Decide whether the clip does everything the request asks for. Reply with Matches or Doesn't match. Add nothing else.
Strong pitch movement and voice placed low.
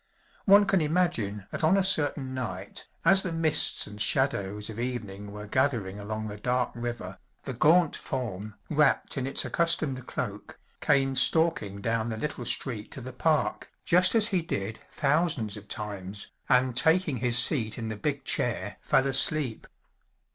Matches